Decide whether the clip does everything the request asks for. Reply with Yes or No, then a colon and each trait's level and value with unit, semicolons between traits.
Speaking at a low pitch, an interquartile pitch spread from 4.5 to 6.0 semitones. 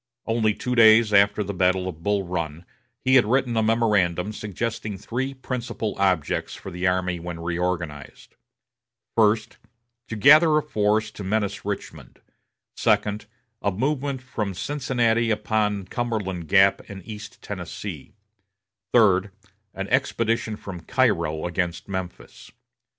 No: low, 105 Hz; average, 4.0 semitones